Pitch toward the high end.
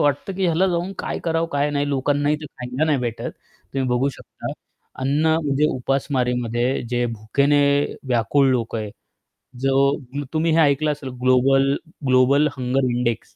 No: low, 135 Hz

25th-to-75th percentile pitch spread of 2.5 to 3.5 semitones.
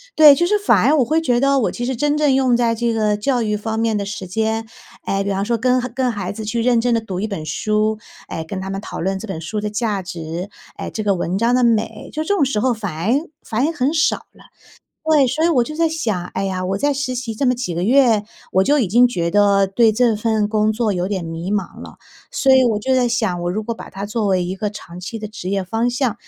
No: average, 4.2 semitones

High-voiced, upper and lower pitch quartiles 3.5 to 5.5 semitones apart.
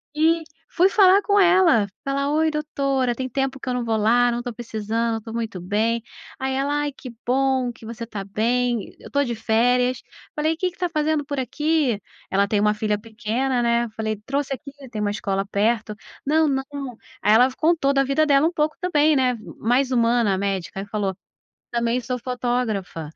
Yes: high, 245 Hz; average, 4.3 semitones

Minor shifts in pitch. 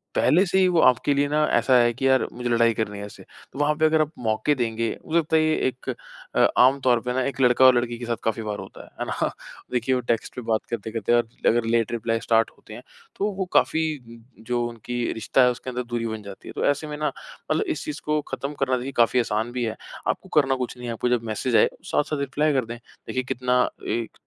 No: average, 3.2 semitones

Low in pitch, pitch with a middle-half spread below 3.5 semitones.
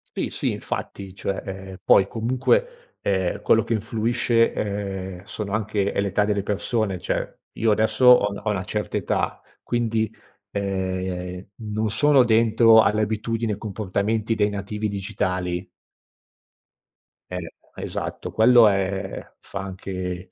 Yes: low, 105 Hz; average, 2.7 semitones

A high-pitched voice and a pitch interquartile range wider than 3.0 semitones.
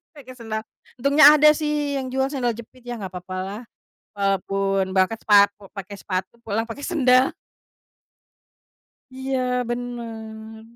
Yes: high, 235 Hz; average, 4.5 semitones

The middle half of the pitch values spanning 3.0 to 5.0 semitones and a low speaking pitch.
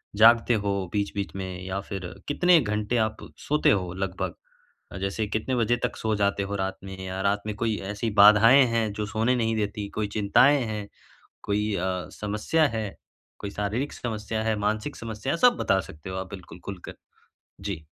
No: narrow, 2.4 semitones; low, 105 Hz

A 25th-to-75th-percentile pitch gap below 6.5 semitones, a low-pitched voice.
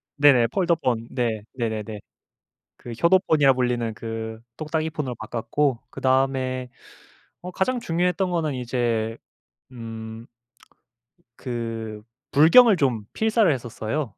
Yes: wide, 5.6 semitones; low, 125 Hz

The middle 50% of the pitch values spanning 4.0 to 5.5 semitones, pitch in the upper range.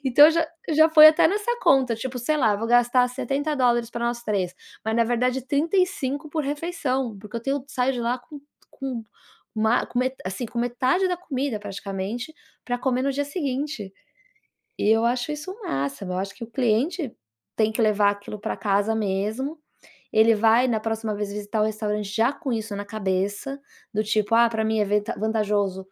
Yes: average, 4.3 semitones; high, 235 Hz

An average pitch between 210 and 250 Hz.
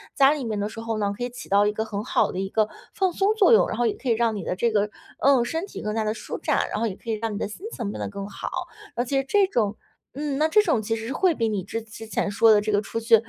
Yes: high, 225 Hz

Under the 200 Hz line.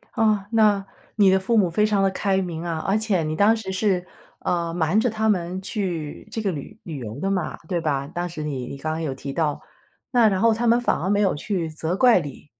Yes: high, 190 Hz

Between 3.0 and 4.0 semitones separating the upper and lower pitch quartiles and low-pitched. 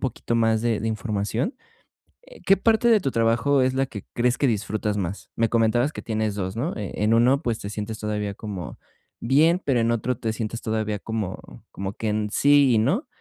Yes: average, 3.6 semitones; low, 115 Hz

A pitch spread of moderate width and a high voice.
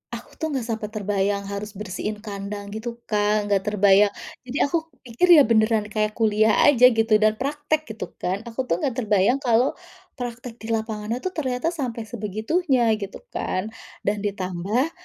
Yes: average, 3.3 semitones; high, 220 Hz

